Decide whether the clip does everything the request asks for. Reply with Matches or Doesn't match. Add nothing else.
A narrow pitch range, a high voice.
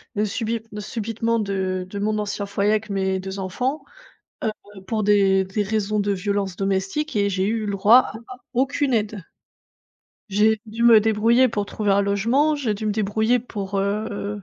Matches